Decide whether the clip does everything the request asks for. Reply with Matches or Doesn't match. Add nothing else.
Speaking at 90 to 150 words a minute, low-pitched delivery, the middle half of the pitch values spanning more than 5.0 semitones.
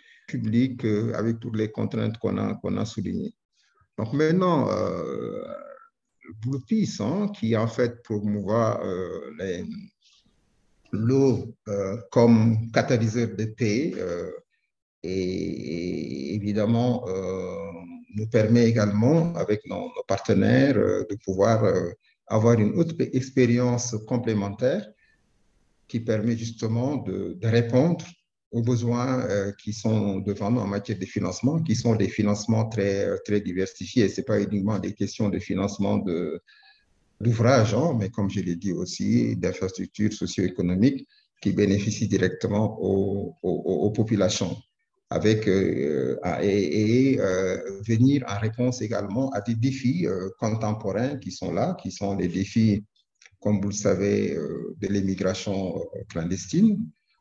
Doesn't match